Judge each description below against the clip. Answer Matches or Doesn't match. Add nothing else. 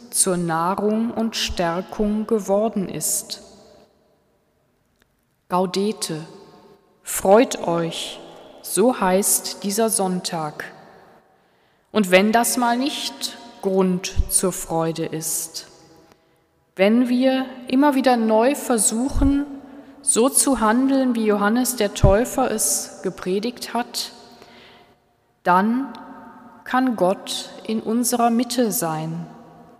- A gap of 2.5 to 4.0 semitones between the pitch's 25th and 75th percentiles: Doesn't match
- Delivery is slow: Matches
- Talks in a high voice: Matches